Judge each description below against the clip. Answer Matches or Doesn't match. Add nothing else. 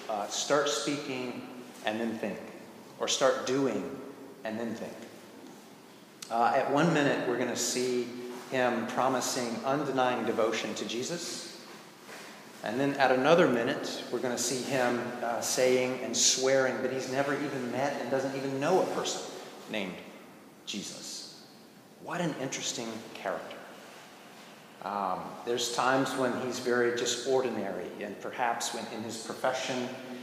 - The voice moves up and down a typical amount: Doesn't match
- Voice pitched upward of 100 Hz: Matches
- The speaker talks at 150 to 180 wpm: Doesn't match